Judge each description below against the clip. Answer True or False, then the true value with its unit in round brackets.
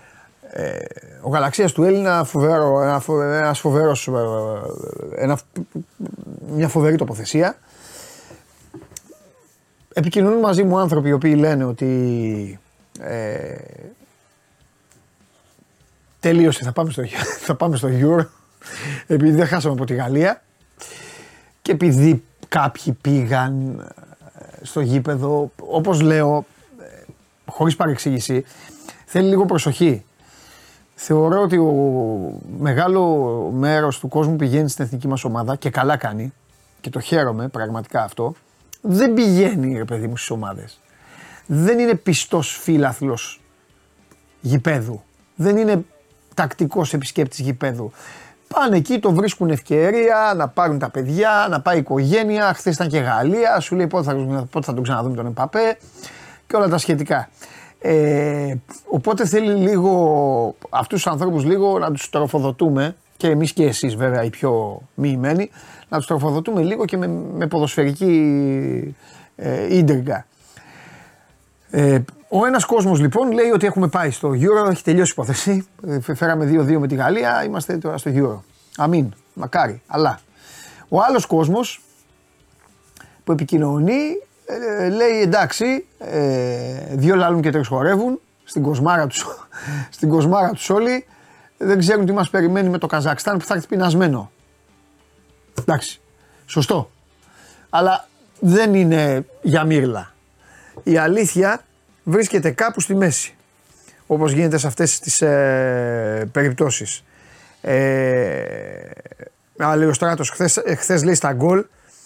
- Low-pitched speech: False (155 Hz)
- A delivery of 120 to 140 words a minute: True (125 wpm)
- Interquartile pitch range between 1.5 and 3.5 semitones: False (5.1 semitones)